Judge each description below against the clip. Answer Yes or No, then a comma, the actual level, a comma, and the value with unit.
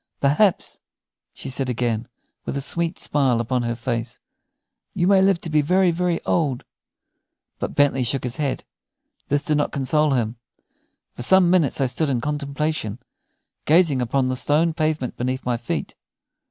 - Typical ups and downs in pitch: Yes, average, 4.2 semitones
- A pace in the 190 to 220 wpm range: No, average, 160 wpm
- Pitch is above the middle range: No, medium, 140 Hz